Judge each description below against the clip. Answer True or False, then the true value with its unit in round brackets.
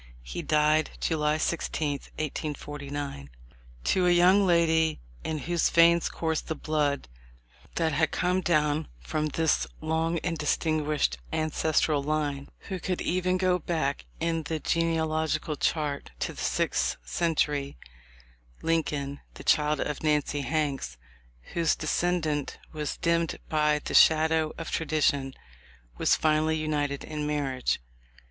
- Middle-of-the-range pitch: True (155 Hz)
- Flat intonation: True (1.9 semitones)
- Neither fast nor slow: False (130 wpm)